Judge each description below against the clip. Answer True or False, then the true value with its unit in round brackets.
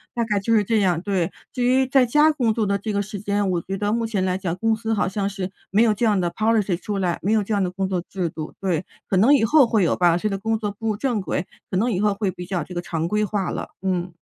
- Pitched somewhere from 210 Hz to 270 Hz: False (200 Hz)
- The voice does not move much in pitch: False (3.2 semitones)